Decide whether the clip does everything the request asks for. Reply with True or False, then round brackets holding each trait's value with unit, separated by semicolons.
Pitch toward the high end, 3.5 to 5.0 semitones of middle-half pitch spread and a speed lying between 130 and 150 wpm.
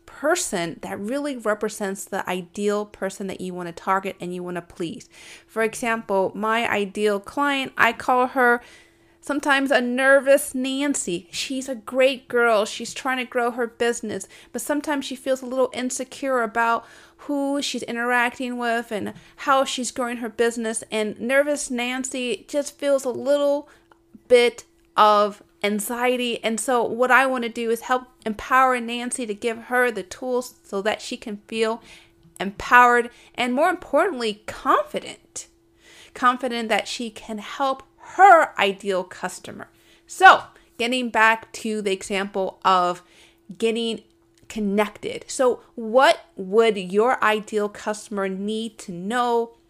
True (235 Hz; 3.9 semitones; 145 wpm)